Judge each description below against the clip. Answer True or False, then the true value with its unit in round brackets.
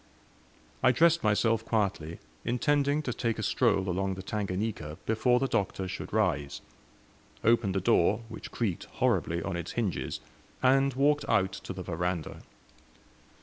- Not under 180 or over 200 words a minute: False (145 wpm)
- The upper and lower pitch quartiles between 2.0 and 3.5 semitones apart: False (4.6 semitones)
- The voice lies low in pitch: True (105 Hz)